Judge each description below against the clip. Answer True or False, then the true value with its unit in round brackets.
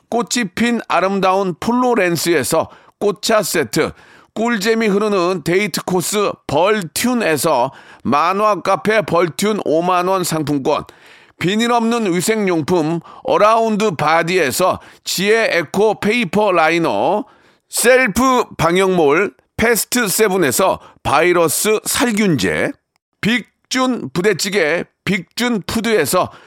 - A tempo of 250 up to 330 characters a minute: False (225 characters per minute)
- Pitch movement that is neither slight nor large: True (4.3 semitones)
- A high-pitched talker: True (205 Hz)